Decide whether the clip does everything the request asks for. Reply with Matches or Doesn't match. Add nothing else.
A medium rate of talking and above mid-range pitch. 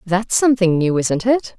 Matches